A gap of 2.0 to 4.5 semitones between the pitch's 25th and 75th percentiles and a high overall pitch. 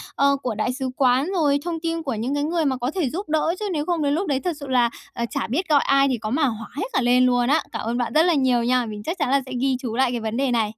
Yes: average, 3.9 semitones; very high, 270 Hz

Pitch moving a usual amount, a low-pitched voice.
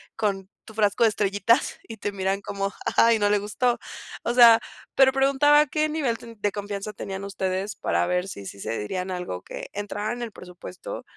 No: average, 3.5 semitones; high, 205 Hz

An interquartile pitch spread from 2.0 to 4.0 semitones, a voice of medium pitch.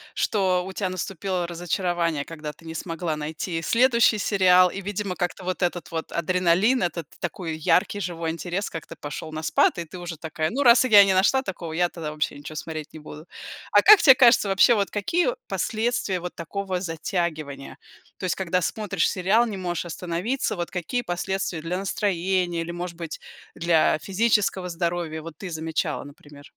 Yes: average, 3.0 semitones; medium, 175 Hz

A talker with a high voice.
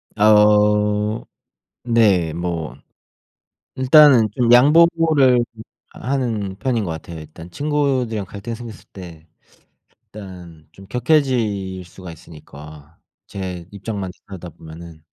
No: low, 105 Hz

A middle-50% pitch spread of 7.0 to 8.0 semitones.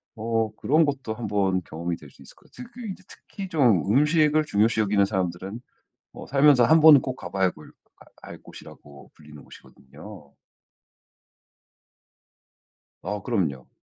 Yes: wide, 7.7 semitones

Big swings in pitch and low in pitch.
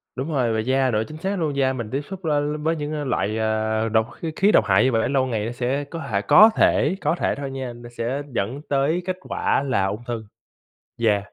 No: average, 4.8 semitones; low, 130 Hz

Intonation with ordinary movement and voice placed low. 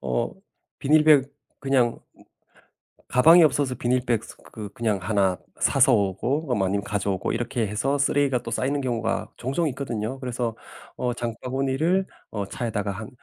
Yes: average, 4.1 semitones; low, 120 Hz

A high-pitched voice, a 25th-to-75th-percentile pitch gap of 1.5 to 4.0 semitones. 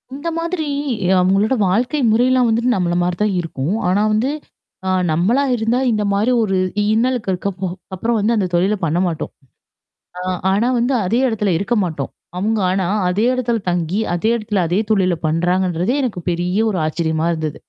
No: high, 200 Hz; average, 4.8 semitones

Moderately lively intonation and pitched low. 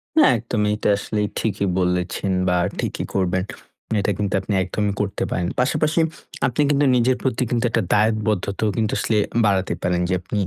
Yes: average, 3.1 semitones; low, 105 Hz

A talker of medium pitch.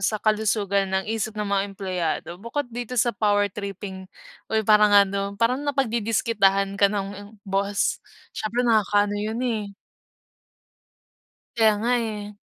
No: high, 205 Hz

